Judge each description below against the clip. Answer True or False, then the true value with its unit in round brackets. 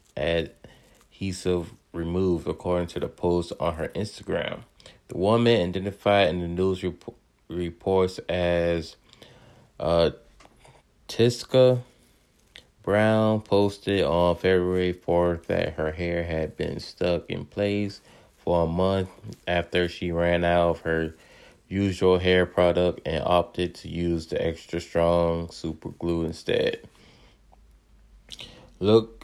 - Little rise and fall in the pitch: True (2.3 semitones)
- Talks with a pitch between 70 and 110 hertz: True (90 Hz)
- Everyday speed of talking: False (115 wpm)